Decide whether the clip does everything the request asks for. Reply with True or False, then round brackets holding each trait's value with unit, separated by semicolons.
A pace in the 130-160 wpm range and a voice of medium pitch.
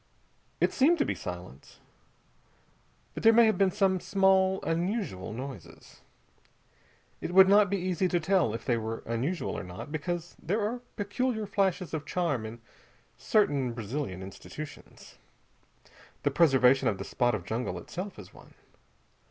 True (150 wpm; 175 Hz)